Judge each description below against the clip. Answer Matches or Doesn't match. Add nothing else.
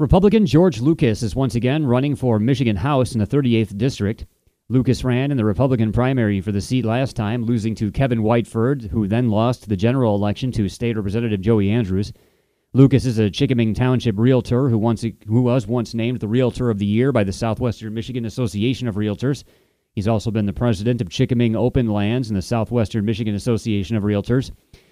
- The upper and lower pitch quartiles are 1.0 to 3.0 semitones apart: Matches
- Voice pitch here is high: Doesn't match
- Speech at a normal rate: Matches